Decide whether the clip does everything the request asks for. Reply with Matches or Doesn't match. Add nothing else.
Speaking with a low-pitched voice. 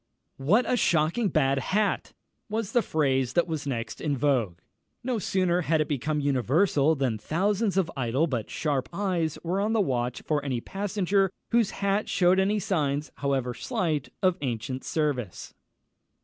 Doesn't match